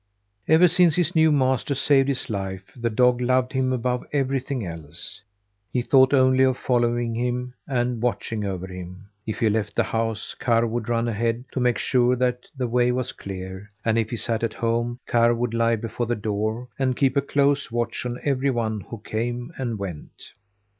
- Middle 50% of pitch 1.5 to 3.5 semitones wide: Yes, narrow, 2.5 semitones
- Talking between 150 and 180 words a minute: No, average, 190 wpm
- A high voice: No, low, 120 Hz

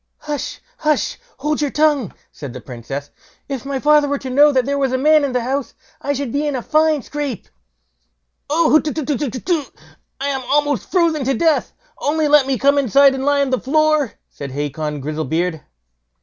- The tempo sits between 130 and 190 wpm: Yes, average, 180 wpm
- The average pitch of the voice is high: Yes, very high, 280 Hz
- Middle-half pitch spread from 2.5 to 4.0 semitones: Yes, average, 2.9 semitones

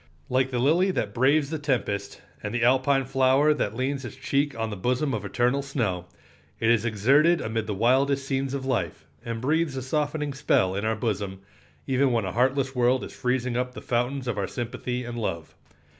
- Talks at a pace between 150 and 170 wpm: No, average, 200 wpm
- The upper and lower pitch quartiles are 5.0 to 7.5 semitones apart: No, average, 3.2 semitones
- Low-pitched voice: Yes, low, 125 Hz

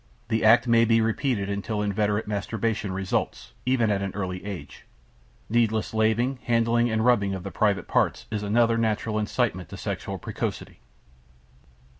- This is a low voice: Yes, low, 110 Hz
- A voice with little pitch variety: Yes, narrow, 2.3 semitones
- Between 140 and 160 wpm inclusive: Yes, average, 150 wpm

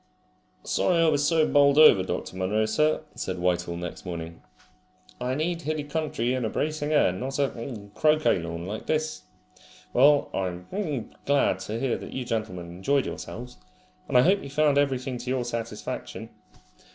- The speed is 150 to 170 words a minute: Yes, average, 165 wpm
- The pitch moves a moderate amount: No, wide, 6.6 semitones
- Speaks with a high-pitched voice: No, low, 130 Hz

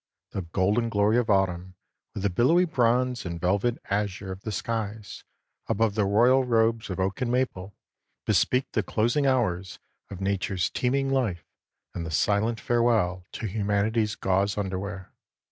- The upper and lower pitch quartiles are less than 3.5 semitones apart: No, average, 3.8 semitones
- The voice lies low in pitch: Yes, low, 105 Hz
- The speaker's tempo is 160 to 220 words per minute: No, average, 150 wpm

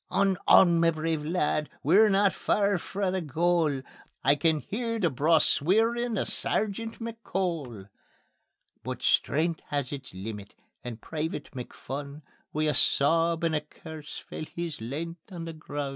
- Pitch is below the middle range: No, medium, 165 Hz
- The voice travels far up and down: No, average, 4.5 semitones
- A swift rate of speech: No, average, 150 wpm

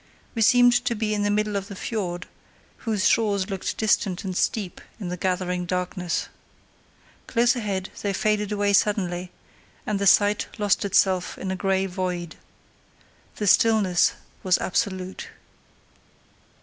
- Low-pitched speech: No, high, 200 Hz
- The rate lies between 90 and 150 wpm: Yes, average, 140 wpm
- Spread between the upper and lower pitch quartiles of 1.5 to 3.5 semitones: Yes, narrow, 2.4 semitones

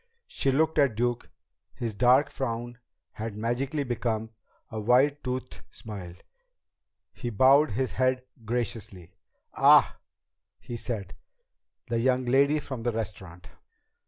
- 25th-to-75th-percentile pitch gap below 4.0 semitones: Yes, average, 2.9 semitones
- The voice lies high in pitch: No, low, 120 Hz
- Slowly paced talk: Yes, slow, 120 wpm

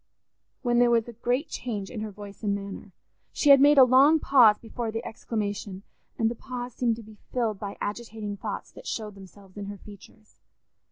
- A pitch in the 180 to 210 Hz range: No, high, 220 Hz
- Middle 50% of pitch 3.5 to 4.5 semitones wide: No, average, 3.1 semitones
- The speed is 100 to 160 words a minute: No, average, 200 wpm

